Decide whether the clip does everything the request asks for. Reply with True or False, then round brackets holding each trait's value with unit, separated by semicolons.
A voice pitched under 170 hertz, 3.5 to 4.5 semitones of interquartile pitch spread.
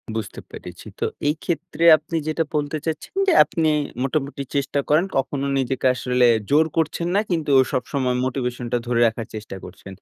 True (140 Hz; 4.0 semitones)